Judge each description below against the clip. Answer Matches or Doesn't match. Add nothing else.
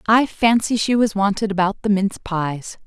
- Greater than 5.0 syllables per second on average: Doesn't match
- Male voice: Doesn't match